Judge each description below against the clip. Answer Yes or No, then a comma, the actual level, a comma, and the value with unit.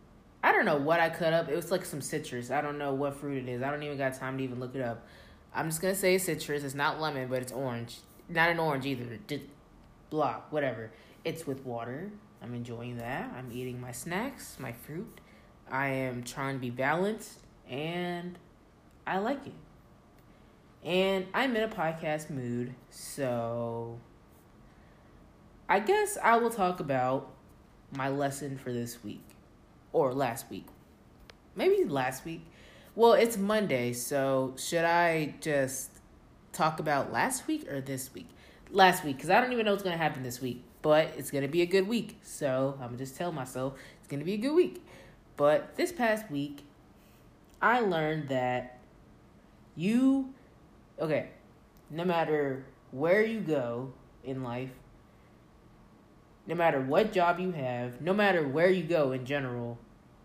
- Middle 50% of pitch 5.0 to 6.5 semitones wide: Yes, wide, 5.5 semitones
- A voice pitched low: No, medium, 145 Hz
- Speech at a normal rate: Yes, average, 170 wpm